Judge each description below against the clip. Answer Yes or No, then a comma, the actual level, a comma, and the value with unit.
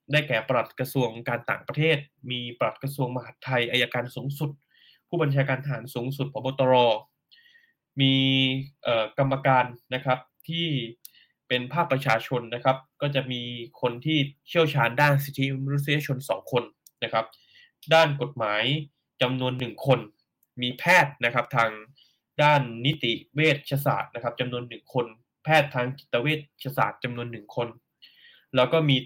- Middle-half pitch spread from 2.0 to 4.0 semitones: Yes, average, 2.9 semitones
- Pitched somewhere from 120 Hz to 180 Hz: Yes, low, 130 Hz